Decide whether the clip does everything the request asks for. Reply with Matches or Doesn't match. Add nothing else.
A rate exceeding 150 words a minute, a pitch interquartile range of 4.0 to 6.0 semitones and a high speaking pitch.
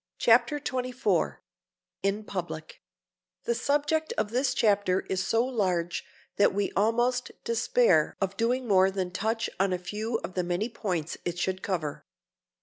Doesn't match